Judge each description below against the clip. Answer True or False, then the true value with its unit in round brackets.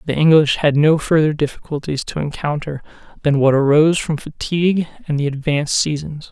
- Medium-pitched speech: True (150 Hz)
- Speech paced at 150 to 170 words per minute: True (160 wpm)